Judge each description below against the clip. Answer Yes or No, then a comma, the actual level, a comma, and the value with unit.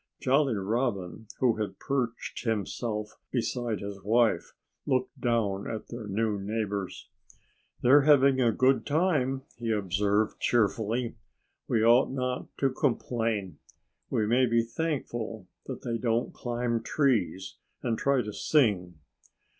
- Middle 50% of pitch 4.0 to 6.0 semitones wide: No, average, 3.3 semitones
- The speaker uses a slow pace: Yes, slow, 125 wpm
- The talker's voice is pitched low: Yes, low, 115 Hz